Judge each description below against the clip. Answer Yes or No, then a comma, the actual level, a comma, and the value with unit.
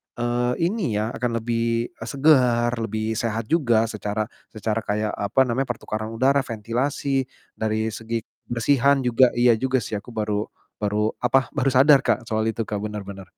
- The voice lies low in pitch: Yes, low, 115 Hz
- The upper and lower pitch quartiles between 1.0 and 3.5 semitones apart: Yes, average, 2.9 semitones